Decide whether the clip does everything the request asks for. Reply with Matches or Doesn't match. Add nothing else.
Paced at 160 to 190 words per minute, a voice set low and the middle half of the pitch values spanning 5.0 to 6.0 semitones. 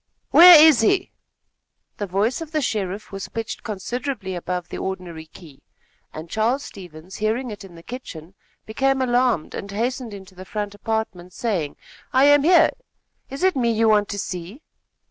Doesn't match